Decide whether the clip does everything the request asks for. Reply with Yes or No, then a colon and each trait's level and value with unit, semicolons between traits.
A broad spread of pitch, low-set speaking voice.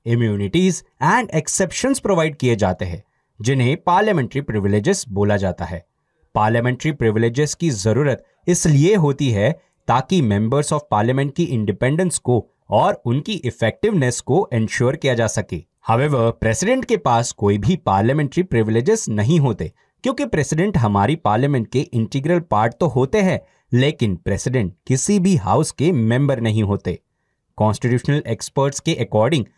Yes: wide, 6.2 semitones; low, 125 Hz